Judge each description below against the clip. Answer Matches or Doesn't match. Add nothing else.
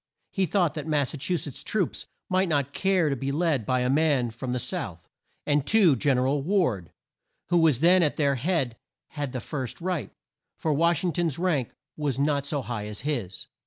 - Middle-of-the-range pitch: Matches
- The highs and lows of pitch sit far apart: Doesn't match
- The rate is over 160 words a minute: Matches